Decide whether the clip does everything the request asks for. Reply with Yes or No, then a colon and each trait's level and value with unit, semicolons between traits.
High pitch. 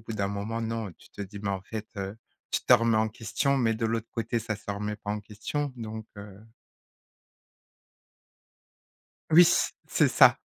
No: low, 110 Hz